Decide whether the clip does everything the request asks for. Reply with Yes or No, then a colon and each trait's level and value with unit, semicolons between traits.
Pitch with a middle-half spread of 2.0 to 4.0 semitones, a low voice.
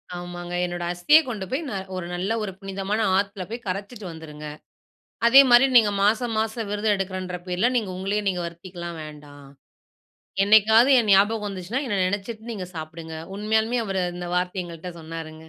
No: average, 3.7 semitones; high, 195 Hz